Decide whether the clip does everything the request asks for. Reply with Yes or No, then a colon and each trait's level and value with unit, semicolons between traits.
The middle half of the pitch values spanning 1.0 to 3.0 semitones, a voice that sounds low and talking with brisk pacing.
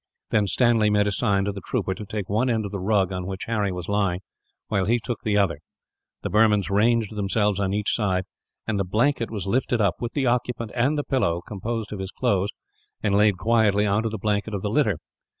Yes: narrow, 2.6 semitones; low, 105 Hz; fast, 225 wpm